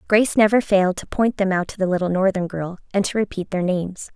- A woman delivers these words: Yes, female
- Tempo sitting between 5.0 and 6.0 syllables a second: No, 6.3 syllables/s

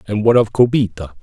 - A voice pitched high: No, low, 110 Hz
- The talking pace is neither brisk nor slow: Yes, average, 195 wpm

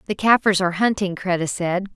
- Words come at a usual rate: Yes, average, 185 wpm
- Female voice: Yes, female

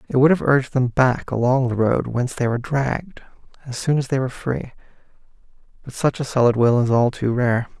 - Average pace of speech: No, fast, 215 wpm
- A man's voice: Yes, male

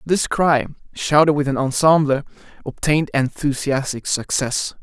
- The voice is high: No, medium, 140 Hz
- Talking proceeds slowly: Yes, slow, 110 wpm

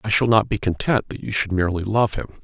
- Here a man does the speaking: Yes, male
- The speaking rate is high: Yes, fast, 270 wpm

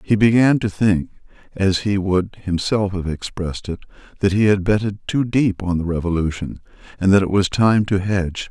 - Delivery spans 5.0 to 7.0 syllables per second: Yes, 5.1 syllables/s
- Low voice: Yes, very low, 95 Hz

